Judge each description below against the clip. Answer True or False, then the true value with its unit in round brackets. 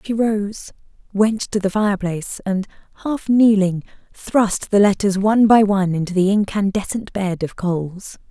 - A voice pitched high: True (200 Hz)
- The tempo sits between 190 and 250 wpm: False (150 wpm)